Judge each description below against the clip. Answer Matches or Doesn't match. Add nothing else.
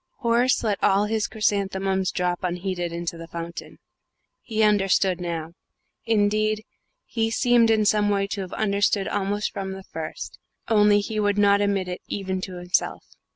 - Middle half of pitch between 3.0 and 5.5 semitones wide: Doesn't match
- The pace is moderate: Matches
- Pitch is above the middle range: Matches